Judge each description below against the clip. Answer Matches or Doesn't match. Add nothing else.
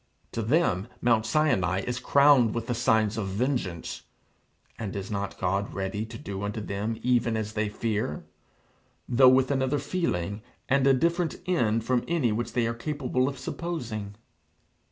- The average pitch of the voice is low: Matches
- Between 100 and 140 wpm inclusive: Doesn't match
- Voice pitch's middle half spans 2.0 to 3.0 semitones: Doesn't match